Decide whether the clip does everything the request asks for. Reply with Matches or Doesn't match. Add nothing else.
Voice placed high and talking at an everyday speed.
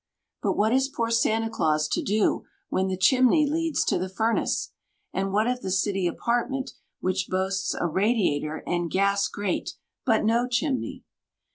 Matches